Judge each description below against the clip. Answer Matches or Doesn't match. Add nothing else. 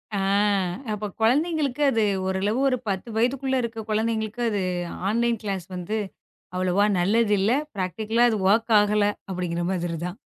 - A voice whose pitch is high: Matches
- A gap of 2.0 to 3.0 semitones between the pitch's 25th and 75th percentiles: Doesn't match